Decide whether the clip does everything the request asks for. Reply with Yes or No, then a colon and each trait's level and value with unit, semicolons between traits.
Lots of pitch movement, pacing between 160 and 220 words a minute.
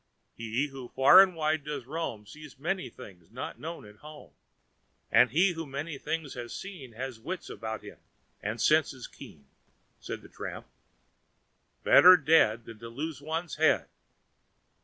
No: wide, 5.7 semitones; average, 150 wpm